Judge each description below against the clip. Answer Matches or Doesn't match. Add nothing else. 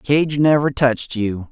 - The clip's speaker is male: Matches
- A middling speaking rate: Matches